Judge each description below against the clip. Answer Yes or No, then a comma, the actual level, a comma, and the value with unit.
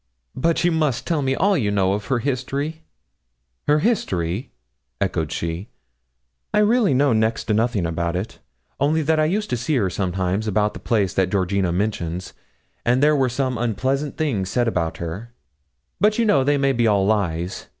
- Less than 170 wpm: No, average, 180 wpm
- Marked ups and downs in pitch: Yes, wide, 7.0 semitones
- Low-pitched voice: Yes, low, 120 Hz